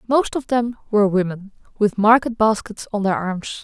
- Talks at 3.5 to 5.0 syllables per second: Yes, 4.9 syllables/s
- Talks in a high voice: Yes, high, 215 Hz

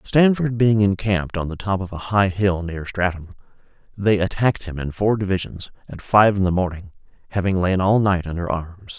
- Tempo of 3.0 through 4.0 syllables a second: No, 5.3 syllables/s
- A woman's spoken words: No, male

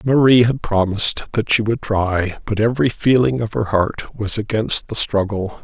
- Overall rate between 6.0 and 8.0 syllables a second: No, 4.7 syllables/s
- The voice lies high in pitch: No, low, 110 Hz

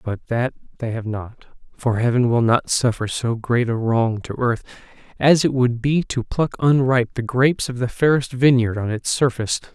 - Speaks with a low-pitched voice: Yes, low, 120 Hz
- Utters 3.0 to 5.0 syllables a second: Yes, 4.9 syllables/s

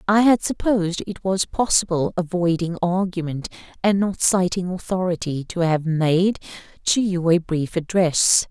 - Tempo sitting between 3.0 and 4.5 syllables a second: Yes, 4.4 syllables/s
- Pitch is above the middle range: No, medium, 180 Hz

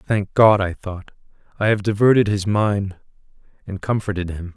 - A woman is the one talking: No, male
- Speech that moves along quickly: No, average, 160 wpm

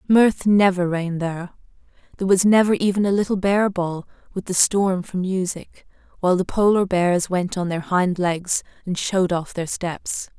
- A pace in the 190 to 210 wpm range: No, average, 180 wpm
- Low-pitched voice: No, medium, 185 Hz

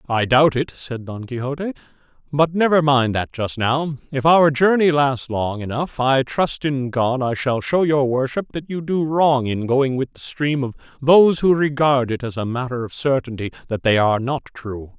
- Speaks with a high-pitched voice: No, low, 135 Hz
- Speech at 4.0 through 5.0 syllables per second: Yes, 4.7 syllables/s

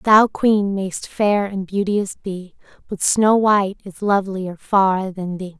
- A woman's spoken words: Yes, female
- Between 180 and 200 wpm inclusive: No, average, 160 wpm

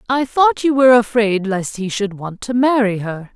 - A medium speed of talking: No, fast, 215 wpm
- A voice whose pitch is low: No, high, 225 Hz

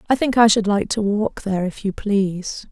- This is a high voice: Yes, high, 210 Hz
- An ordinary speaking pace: No, fast, 245 wpm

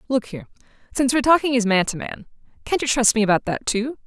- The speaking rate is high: Yes, fast, 235 wpm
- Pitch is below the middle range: No, high, 240 Hz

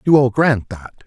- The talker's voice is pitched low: Yes, low, 125 Hz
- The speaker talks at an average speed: No, fast, 225 wpm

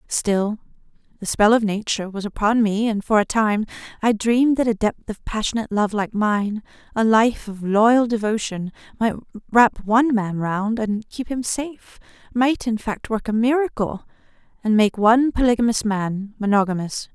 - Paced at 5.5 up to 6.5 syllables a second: No, 4.7 syllables/s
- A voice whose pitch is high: Yes, high, 220 Hz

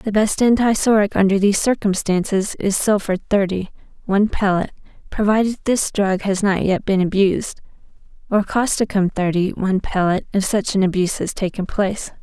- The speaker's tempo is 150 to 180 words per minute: Yes, average, 155 wpm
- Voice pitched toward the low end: No, high, 200 Hz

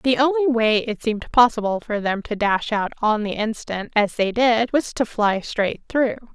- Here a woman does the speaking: Yes, female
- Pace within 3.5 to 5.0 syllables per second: Yes, 4.5 syllables/s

